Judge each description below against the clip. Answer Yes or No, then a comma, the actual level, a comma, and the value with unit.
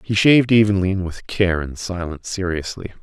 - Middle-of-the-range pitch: No, very low, 95 Hz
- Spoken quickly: No, average, 180 wpm